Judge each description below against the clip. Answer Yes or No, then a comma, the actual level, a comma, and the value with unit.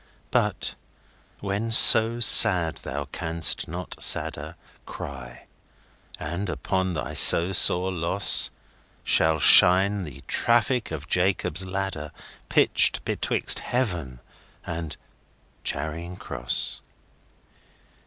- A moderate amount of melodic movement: Yes, average, 4.0 semitones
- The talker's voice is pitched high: No, very low, 90 Hz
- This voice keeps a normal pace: No, slow, 80 wpm